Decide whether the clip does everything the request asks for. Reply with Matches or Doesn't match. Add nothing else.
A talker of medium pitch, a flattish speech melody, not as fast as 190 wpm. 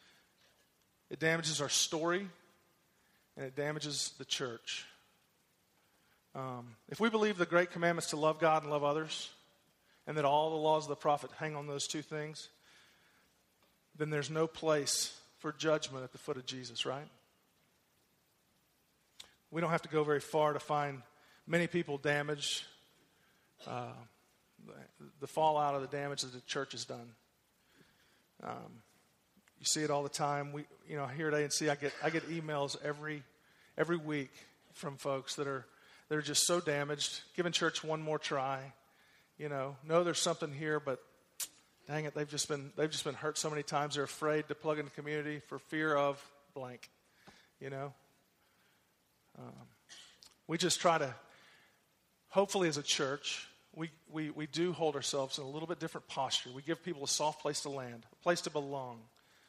Matches